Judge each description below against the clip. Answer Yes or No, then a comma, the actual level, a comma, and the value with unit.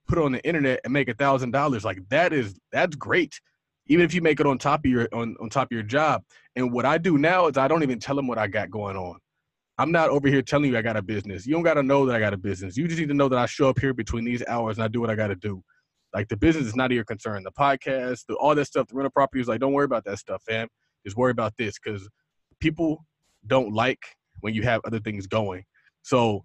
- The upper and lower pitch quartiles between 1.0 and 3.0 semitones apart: No, average, 4.1 semitones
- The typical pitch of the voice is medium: No, low, 125 Hz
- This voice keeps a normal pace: No, fast, 285 wpm